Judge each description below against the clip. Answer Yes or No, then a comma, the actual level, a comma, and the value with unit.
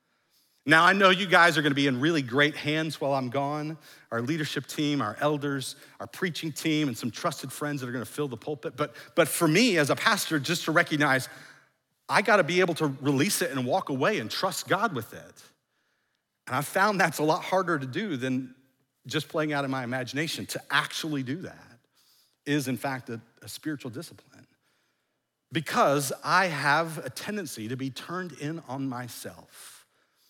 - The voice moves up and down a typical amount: Yes, average, 3.3 semitones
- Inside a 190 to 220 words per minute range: Yes, average, 195 wpm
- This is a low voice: No, medium, 145 Hz